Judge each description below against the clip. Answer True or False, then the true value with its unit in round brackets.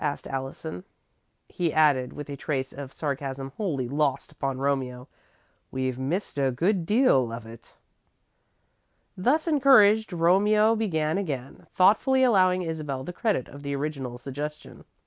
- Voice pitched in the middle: True (150 Hz)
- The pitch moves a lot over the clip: True (6.2 semitones)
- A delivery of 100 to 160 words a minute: True (135 wpm)